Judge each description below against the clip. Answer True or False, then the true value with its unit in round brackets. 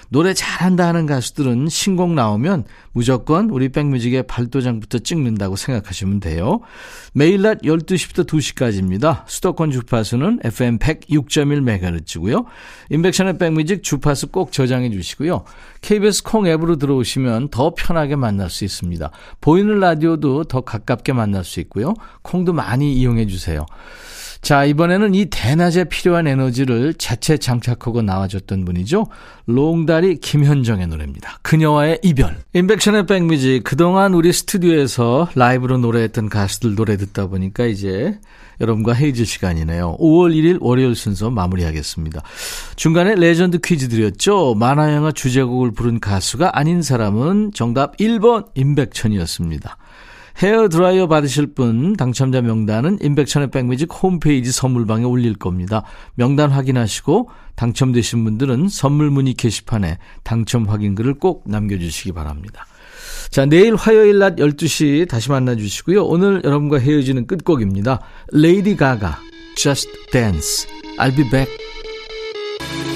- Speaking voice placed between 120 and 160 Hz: True (135 Hz)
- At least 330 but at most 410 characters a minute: True (340 characters per minute)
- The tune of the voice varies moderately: False (6.9 semitones)